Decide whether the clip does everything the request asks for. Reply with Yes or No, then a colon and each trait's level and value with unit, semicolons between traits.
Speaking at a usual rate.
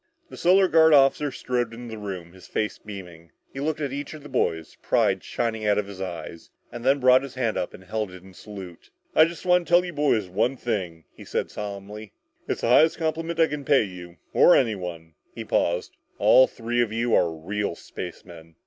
No: fast, 210 wpm